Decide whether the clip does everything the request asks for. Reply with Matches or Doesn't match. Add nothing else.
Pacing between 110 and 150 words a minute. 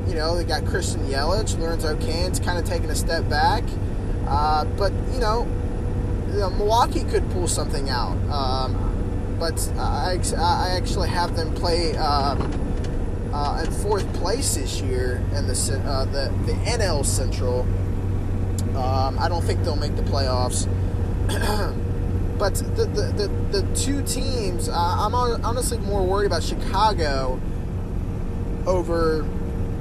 Matches